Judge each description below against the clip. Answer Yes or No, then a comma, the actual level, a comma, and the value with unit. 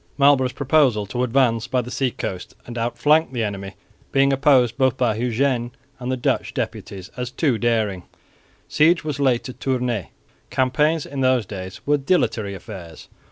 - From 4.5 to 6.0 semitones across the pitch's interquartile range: No, average, 3.5 semitones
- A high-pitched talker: No, low, 125 Hz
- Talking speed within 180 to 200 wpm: No, average, 160 wpm